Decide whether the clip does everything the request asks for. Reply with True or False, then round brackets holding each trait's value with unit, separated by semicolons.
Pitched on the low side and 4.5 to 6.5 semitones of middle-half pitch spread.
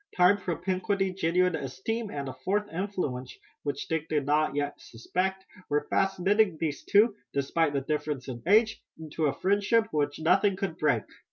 False (165 Hz; 5.1 semitones)